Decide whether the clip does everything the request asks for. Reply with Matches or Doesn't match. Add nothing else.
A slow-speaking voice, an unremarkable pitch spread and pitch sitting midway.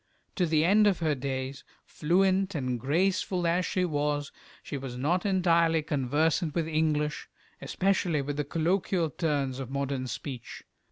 Doesn't match